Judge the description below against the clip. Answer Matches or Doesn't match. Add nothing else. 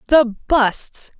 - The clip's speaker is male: Doesn't match